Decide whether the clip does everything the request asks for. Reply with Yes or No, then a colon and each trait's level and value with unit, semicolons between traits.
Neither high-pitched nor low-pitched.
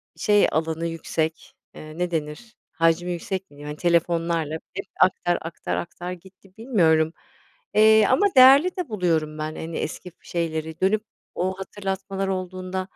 Yes: medium, 175 Hz